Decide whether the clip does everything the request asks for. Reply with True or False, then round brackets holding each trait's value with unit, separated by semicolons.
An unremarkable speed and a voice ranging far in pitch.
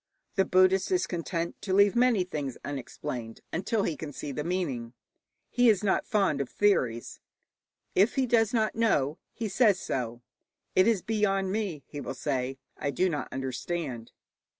True (165 wpm; 7.0 semitones)